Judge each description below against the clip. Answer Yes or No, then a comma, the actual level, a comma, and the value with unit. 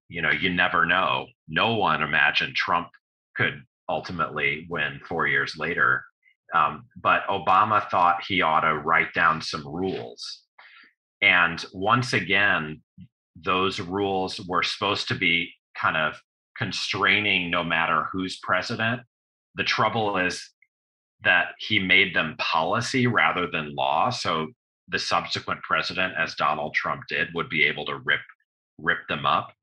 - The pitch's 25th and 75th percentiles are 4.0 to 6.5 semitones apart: Yes, average, 4.5 semitones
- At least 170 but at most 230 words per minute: No, average, 140 wpm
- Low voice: Yes, very low, 90 Hz